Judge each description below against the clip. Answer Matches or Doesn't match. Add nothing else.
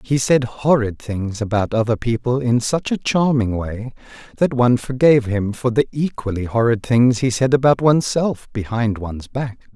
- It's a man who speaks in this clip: Matches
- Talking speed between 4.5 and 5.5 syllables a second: Matches